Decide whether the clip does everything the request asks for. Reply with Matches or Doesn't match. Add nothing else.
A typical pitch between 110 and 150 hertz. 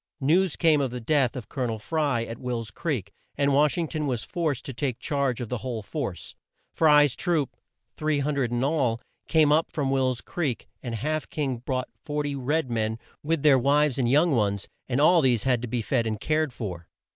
Matches